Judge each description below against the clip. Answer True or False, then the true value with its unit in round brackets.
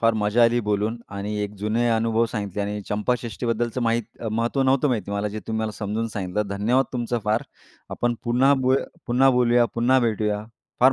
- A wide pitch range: False (2.4 semitones)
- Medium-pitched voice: False (115 Hz)